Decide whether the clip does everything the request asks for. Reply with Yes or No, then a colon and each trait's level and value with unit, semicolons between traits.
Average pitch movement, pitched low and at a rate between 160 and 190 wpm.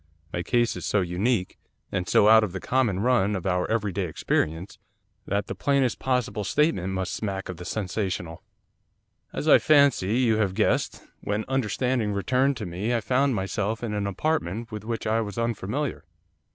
Yes: average, 4.4 semitones; low, 105 Hz; average, 180 wpm